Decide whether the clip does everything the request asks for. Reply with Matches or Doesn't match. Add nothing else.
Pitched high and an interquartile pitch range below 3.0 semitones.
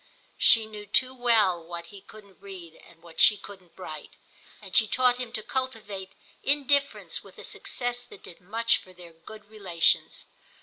Doesn't match